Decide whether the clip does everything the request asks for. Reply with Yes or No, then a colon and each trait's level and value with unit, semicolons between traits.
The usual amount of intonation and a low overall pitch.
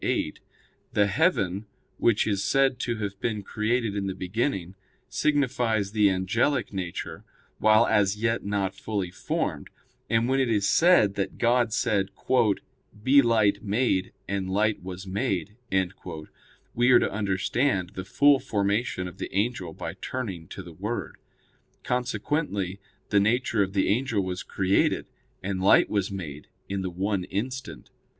Yes: average, 3.8 semitones; low, 105 Hz